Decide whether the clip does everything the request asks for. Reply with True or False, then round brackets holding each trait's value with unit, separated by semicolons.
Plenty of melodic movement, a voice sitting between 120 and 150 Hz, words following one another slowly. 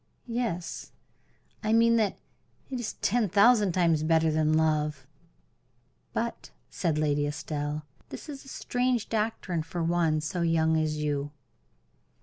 False (6.1 semitones; 165 Hz; 130 wpm)